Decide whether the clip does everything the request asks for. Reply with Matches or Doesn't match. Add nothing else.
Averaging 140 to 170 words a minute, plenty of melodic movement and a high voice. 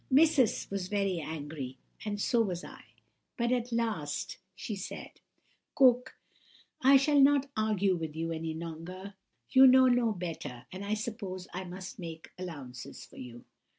Matches